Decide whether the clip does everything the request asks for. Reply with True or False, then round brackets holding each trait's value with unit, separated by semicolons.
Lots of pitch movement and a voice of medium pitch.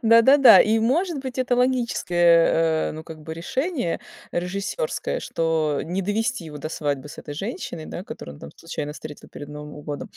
True (8.1 semitones; 175 Hz)